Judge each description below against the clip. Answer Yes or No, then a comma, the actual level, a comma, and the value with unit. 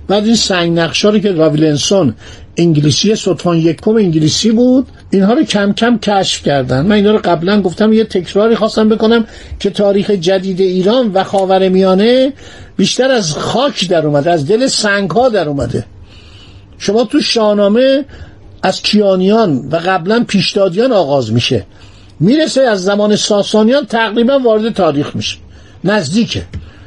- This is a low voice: No, high, 200 Hz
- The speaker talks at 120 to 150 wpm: Yes, average, 145 wpm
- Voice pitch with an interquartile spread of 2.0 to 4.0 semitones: No, wide, 5.6 semitones